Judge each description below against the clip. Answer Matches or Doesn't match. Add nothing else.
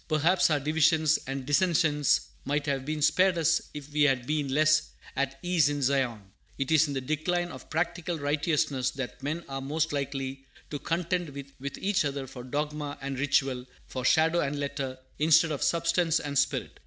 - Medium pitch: Matches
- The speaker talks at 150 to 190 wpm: Matches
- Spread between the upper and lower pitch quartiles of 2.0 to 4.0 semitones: Matches